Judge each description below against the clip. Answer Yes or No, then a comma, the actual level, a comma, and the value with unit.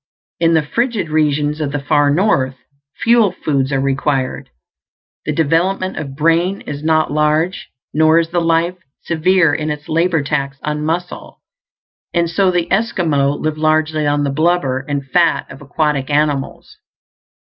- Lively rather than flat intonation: No, average, 2.7 semitones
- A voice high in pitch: No, medium, 155 Hz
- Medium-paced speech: Yes, average, 150 wpm